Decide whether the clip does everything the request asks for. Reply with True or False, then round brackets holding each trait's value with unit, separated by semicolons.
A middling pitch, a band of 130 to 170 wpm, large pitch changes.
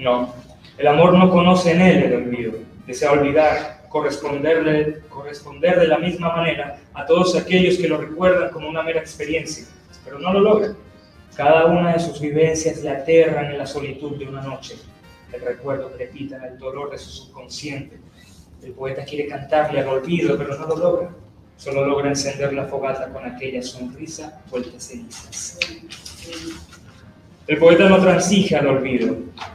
False (145 Hz; 160 wpm; 3.9 semitones)